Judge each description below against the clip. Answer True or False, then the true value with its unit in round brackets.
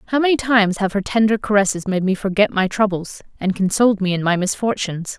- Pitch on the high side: True (200 Hz)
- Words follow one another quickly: True (210 wpm)